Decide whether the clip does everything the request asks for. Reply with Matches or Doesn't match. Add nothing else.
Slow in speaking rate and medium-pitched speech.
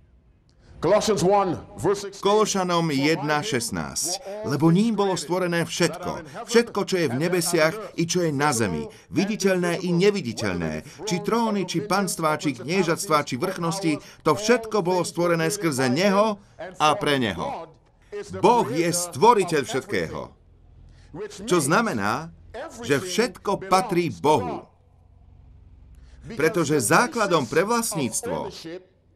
Matches